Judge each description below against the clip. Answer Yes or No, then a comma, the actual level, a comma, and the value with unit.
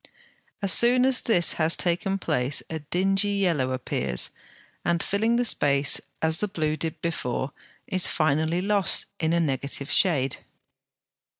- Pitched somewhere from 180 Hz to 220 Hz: No, medium, 165 Hz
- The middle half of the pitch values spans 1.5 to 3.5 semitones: No, average, 5.2 semitones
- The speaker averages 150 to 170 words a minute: No, average, 140 wpm